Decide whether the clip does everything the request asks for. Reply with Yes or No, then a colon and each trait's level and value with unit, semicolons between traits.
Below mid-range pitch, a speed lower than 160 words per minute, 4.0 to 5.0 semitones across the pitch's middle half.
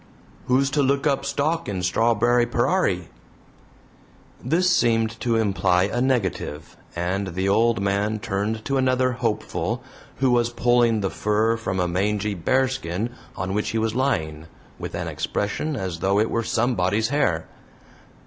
Yes: low, 110 Hz; average, 150 wpm; average, 4.4 semitones